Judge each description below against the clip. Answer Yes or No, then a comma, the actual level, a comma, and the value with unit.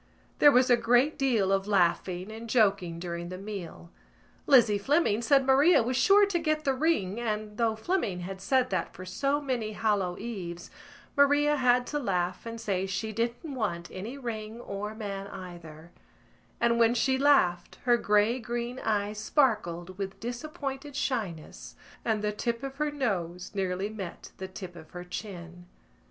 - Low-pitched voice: No, high, 215 Hz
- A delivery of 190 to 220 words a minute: No, average, 165 wpm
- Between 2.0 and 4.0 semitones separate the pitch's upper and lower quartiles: No, wide, 5.5 semitones